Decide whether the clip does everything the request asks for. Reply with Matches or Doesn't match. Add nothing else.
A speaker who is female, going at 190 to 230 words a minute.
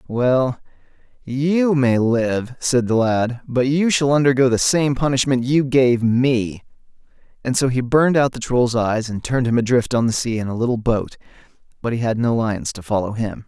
Doesn't match